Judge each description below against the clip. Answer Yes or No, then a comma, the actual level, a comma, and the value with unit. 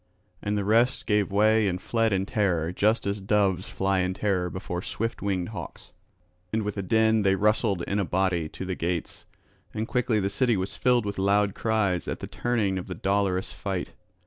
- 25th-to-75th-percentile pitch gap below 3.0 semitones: Yes, narrow, 2.5 semitones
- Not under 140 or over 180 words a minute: No, average, 200 wpm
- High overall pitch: No, low, 100 Hz